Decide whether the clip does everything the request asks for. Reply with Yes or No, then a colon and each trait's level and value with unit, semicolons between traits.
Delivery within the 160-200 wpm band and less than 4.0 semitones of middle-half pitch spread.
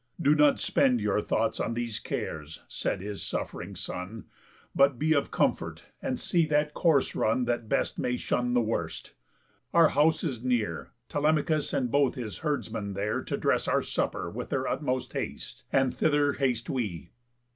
No: average, 165 wpm; average, 4.9 semitones